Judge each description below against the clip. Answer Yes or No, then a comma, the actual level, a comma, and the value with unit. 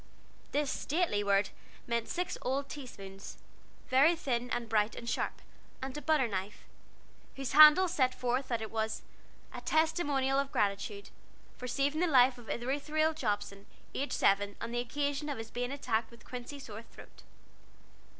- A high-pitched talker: Yes, very high, 255 Hz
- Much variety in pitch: No, average, 4.4 semitones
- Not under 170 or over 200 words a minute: No, average, 160 wpm